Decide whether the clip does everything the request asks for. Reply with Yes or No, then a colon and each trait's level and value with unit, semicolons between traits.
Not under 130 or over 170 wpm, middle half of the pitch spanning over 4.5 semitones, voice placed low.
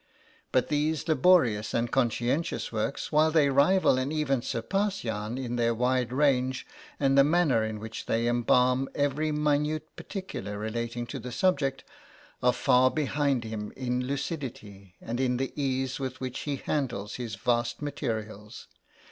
No: average, 150 wpm; average, 3.6 semitones; low, 130 Hz